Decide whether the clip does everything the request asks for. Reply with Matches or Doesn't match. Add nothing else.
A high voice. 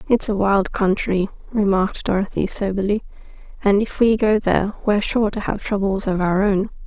Matches